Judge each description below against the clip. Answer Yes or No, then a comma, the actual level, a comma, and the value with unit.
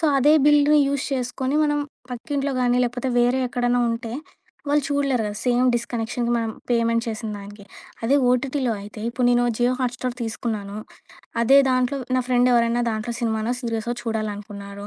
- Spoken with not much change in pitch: Yes, narrow, 2.1 semitones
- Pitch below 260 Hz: Yes, high, 240 Hz